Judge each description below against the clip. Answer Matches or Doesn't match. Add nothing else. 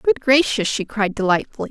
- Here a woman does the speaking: Matches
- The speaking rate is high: Doesn't match